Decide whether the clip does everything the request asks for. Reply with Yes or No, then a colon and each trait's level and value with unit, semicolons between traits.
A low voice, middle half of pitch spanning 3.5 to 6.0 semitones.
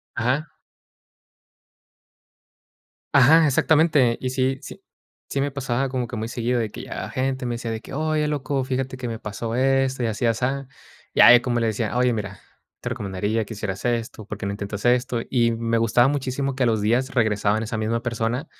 No: low, 120 Hz; average, 2.8 semitones